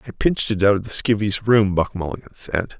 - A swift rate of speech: Yes, fast, 235 wpm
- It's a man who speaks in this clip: Yes, male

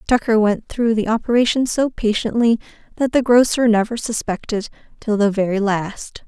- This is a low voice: No, high, 225 Hz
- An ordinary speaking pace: Yes, average, 155 wpm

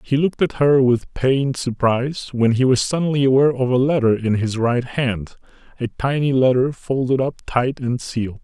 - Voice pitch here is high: No, low, 130 Hz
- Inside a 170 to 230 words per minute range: Yes, average, 190 wpm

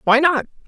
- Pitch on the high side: Yes, very high, 280 Hz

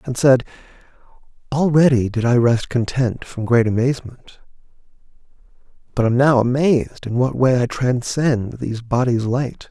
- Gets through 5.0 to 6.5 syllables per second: No, 4.7 syllables/s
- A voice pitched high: No, low, 125 Hz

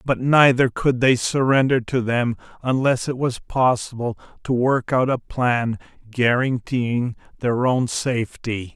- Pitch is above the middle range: No, low, 125 Hz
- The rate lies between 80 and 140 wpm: Yes, slow, 135 wpm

